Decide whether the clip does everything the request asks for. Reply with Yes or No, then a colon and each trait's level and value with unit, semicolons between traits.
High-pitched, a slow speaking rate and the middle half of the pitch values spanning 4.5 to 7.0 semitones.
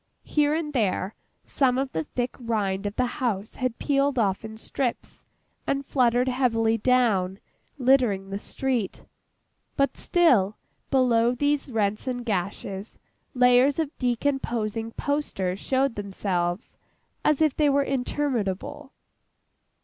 Yes: high, 245 Hz; slow, 125 wpm; average, 4.8 semitones